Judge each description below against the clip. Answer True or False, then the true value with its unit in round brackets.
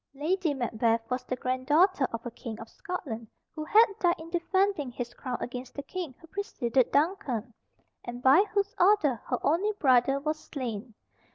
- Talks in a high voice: True (275 Hz)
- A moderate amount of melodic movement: False (6.3 semitones)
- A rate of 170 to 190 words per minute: True (175 wpm)